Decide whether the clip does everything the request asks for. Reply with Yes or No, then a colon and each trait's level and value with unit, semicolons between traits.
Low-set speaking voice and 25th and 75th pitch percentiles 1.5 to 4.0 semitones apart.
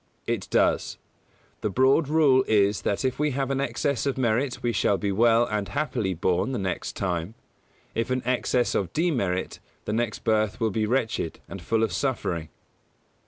No: low, 115 Hz; average, 4.8 semitones